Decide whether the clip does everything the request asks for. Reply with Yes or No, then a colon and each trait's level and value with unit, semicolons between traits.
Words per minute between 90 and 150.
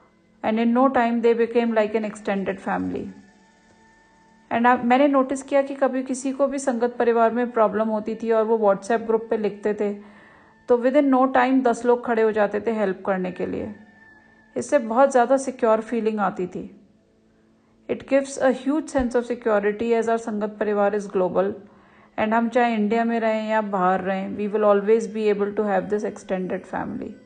No: average, 185 wpm